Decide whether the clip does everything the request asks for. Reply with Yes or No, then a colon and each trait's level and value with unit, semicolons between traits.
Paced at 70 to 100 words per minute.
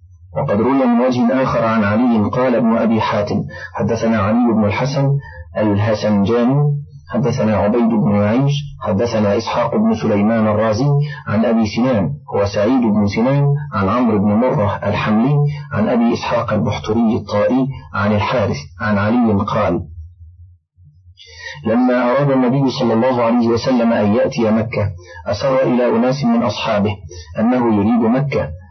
No: fast, 135 wpm